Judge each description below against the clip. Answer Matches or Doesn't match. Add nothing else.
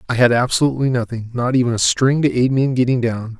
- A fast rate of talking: Matches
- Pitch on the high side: Doesn't match